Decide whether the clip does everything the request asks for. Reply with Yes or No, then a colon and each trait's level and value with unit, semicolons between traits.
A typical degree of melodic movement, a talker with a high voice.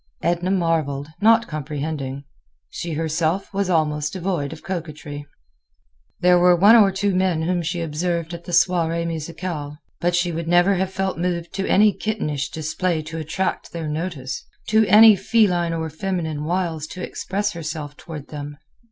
No: average, 3.1 semitones; medium, 170 Hz